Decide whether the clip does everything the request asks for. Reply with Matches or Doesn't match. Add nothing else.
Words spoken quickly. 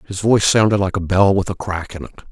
Matches